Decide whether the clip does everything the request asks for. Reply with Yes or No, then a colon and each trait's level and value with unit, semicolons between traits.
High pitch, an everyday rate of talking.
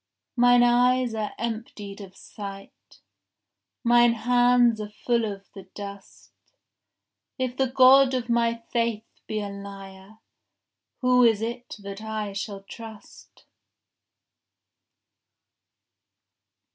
No: high, 225 Hz; slow, 105 wpm